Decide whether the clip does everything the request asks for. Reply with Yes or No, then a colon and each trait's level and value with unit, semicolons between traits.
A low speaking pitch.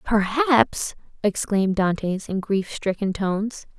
No: high, 205 Hz